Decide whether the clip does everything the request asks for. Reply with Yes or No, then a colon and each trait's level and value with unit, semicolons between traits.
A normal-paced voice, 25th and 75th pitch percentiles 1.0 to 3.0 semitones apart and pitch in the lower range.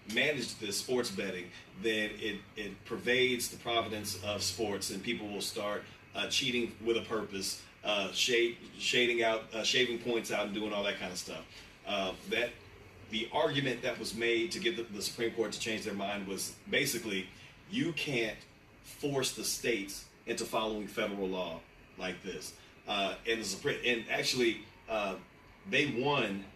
Yes: average, 170 wpm; narrow, 2.6 semitones; low, 110 Hz